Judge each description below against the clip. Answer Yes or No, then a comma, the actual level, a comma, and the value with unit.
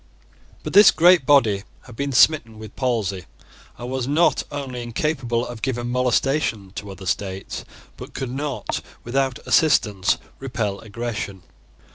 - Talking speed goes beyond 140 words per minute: No, slow, 135 wpm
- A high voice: No, low, 120 Hz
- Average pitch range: Yes, average, 4.4 semitones